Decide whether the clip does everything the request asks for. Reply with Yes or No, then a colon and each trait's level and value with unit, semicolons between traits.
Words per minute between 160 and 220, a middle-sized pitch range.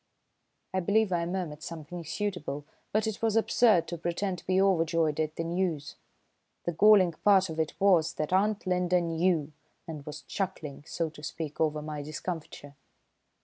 Yes: average, 165 wpm; average, 3.4 semitones